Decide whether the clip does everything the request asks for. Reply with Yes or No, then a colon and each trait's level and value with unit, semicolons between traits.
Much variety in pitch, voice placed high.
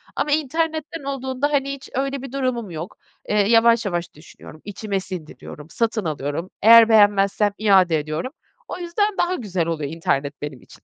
Yes: wide, 8.4 semitones; high, 215 Hz